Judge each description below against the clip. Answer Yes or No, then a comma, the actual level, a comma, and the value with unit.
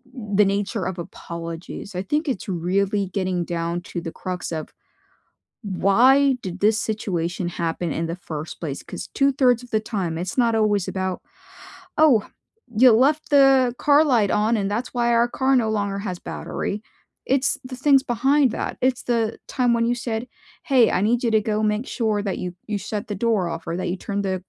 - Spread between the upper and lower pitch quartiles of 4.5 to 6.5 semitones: Yes, average, 4.8 semitones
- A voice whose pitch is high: Yes, high, 210 Hz